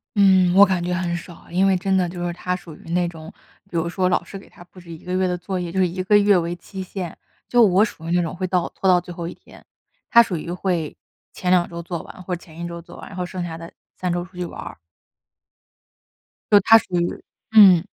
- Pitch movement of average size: No, narrow, 1.6 semitones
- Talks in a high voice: No, medium, 180 Hz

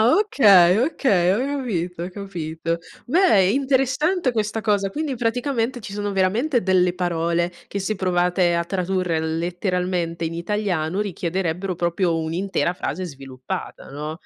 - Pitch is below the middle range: No, medium, 185 Hz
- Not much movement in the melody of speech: No, average, 4.3 semitones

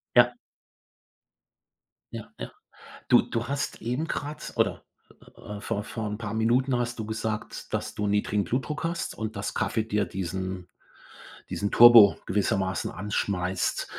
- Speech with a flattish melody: No, average, 3.0 semitones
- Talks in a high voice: No, low, 110 Hz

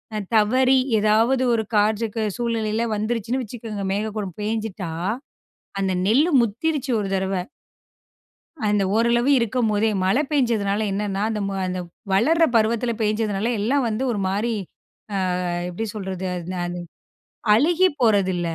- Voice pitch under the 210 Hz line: No, high, 215 Hz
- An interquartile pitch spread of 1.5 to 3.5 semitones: Yes, average, 2.9 semitones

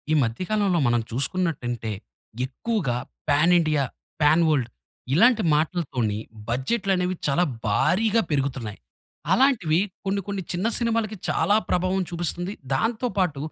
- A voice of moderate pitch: Yes, medium, 175 Hz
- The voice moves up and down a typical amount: No, wide, 6.6 semitones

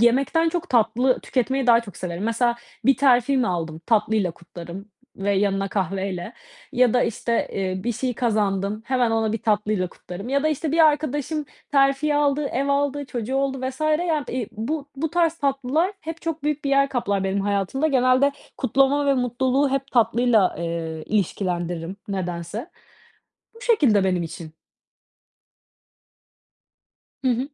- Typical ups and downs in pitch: No, wide, 5.9 semitones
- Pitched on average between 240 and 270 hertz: Yes, high, 245 Hz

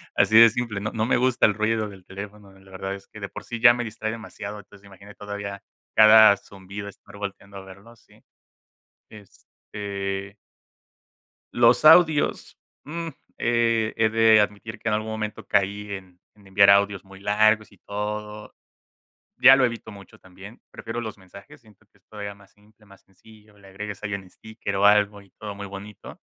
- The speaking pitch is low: Yes, low, 105 Hz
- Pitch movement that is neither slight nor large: No, narrow, 1.7 semitones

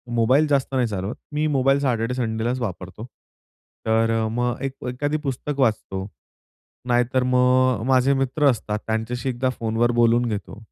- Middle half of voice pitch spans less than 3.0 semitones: Yes, narrow, 2.6 semitones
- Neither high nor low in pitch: No, low, 125 Hz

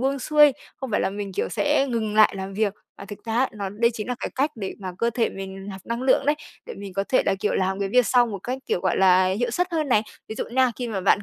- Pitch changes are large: No, average, 4.4 semitones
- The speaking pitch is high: Yes, high, 215 Hz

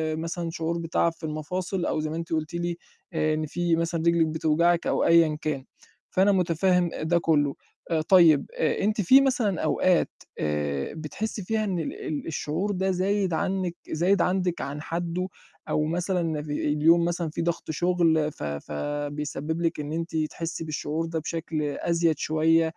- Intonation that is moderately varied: No, narrow, 2.3 semitones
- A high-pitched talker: No, medium, 165 Hz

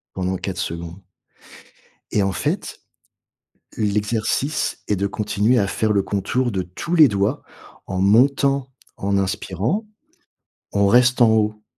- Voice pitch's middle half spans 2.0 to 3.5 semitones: No, average, 4.1 semitones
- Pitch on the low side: Yes, low, 105 Hz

